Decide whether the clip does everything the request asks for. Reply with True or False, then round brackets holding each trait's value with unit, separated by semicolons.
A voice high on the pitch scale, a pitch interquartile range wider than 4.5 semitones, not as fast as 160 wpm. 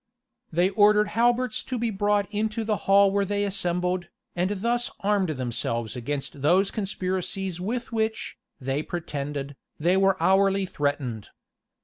True (195 Hz; 4.9 semitones; 135 wpm)